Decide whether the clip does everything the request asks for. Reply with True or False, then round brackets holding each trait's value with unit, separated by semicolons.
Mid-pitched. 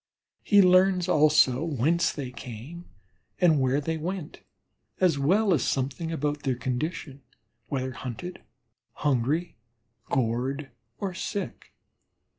True (150 Hz)